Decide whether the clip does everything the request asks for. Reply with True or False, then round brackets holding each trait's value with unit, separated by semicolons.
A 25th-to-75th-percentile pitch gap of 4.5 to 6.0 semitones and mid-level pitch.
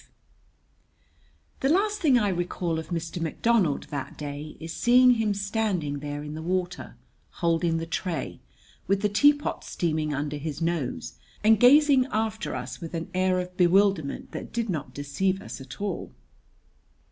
True (5.6 semitones; 180 Hz)